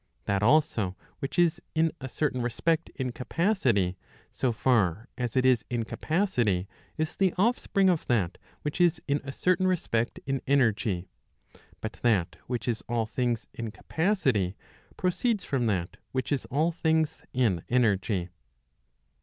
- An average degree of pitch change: No, wide, 6.5 semitones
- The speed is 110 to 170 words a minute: Yes, average, 145 wpm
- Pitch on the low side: Yes, low, 125 Hz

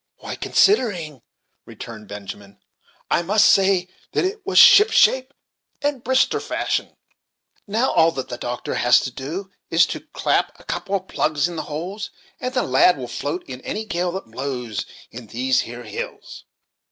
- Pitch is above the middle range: No, medium, 165 Hz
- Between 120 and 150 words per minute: No, average, 165 wpm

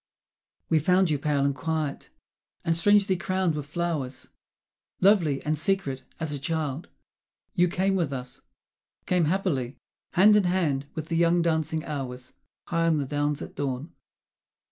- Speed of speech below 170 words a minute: Yes, average, 150 wpm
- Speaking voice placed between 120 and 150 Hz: No, medium, 160 Hz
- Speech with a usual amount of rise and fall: Yes, average, 3.9 semitones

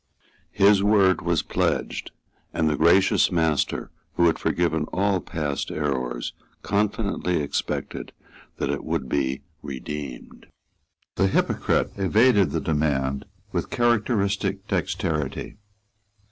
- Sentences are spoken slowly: Yes, slow, 105 wpm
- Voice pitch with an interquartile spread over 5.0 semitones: Yes, wide, 5.6 semitones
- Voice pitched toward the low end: Yes, very low, 85 Hz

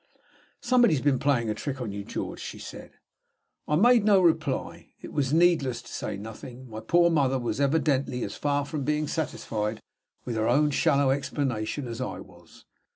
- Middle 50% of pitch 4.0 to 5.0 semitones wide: Yes, average, 4.3 semitones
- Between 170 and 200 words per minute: Yes, average, 180 wpm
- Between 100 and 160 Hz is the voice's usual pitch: Yes, medium, 140 Hz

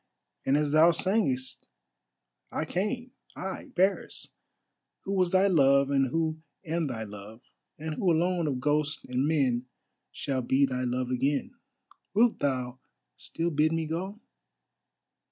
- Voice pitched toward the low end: No, medium, 150 Hz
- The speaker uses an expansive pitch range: No, average, 4.8 semitones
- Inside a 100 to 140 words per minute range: Yes, slow, 135 wpm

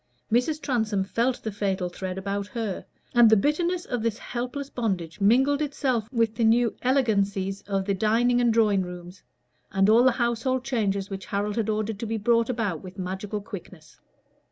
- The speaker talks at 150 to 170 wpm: No, average, 180 wpm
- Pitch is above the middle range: Yes, high, 220 Hz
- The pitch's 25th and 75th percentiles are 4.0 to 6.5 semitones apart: No, average, 3.6 semitones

